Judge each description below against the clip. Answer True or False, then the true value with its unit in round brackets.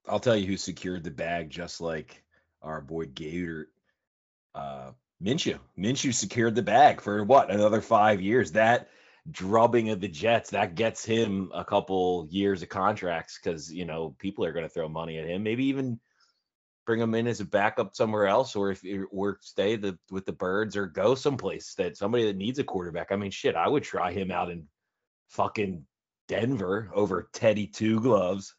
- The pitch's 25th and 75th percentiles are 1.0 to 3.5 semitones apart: False (4.0 semitones)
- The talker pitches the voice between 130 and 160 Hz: False (100 Hz)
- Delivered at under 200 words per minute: True (190 wpm)